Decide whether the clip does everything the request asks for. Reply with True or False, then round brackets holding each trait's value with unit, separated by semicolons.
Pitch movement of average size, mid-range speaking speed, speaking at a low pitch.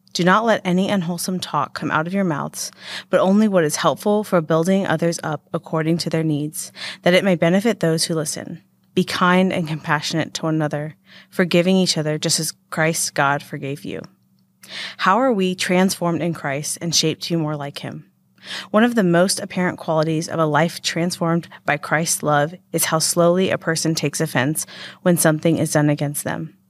False (3.0 semitones; 190 wpm; 165 Hz)